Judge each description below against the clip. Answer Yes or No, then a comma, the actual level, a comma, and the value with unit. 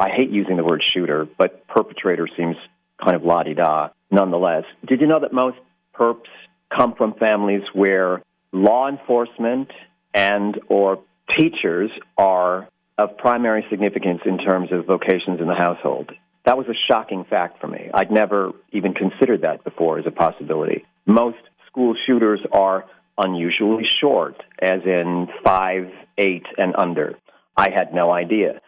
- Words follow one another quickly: No, average, 145 wpm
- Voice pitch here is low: Yes, low, 100 Hz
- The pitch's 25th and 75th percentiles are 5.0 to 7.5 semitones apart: No, average, 4.1 semitones